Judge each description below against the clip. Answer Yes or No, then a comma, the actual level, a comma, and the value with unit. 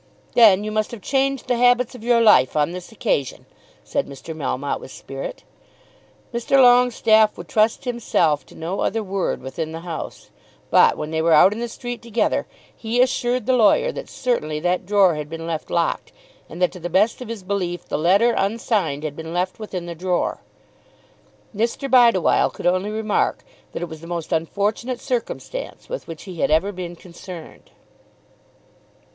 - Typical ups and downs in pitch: No, wide, 5.9 semitones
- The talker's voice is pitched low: No, high, 200 Hz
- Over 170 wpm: Yes, average, 180 wpm